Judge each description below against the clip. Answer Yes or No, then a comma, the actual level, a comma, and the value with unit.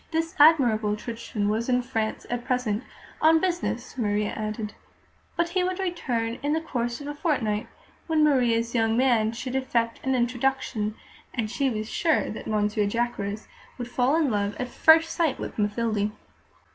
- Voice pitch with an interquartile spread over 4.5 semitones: Yes, average, 4.9 semitones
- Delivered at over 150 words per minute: Yes, average, 165 wpm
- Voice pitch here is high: Yes, high, 240 Hz